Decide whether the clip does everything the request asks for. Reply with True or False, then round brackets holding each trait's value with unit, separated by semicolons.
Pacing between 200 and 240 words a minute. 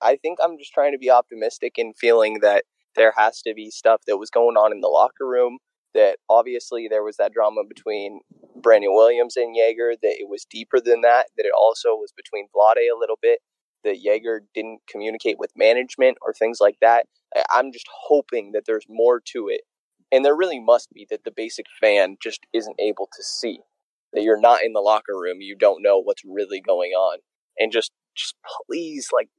True (205 wpm)